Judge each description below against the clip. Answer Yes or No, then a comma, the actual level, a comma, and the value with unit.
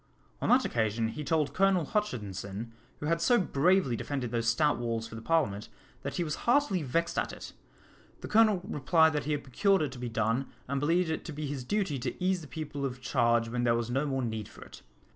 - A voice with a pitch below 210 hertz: Yes, medium, 140 Hz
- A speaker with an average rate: No, fast, 225 wpm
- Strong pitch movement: Yes, wide, 6.1 semitones